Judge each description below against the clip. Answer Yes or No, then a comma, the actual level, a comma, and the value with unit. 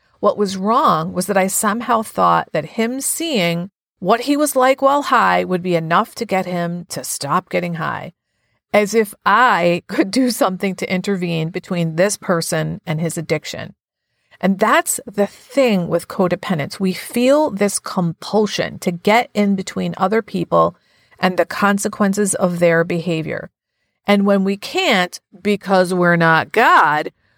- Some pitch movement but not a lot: Yes, average, 3.8 semitones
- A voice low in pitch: No, high, 190 Hz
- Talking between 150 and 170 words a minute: Yes, average, 155 wpm